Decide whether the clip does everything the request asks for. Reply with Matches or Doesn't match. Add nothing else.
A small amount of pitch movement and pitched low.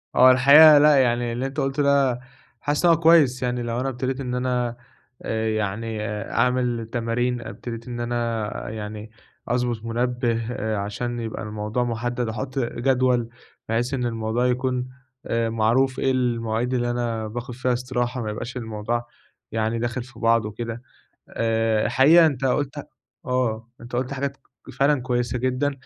Matches